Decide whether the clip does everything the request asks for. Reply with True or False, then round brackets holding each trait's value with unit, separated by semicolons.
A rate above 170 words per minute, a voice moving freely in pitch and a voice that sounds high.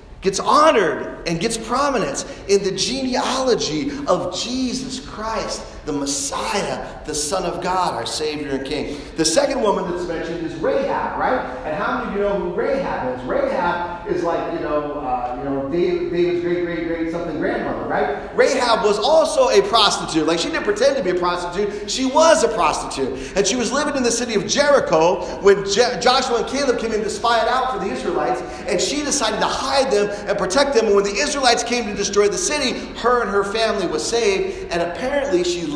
True (200 wpm; 7.1 semitones; 205 Hz)